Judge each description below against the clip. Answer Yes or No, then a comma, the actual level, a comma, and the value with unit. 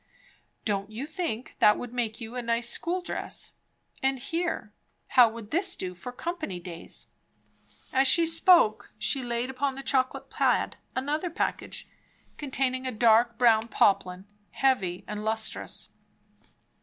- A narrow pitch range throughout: No, average, 3.9 semitones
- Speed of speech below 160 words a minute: Yes, average, 140 wpm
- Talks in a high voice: Yes, high, 245 Hz